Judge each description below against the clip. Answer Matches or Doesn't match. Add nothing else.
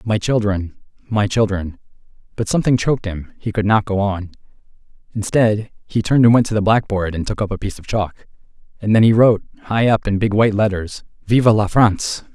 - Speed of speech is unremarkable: Matches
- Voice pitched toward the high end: Doesn't match